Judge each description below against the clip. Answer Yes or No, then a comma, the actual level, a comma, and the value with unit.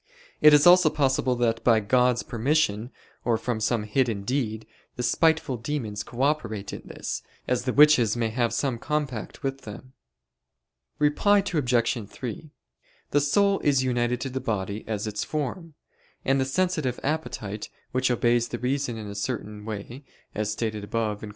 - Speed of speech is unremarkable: Yes, average, 165 wpm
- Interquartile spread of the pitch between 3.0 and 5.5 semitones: Yes, average, 4.4 semitones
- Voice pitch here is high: No, low, 125 Hz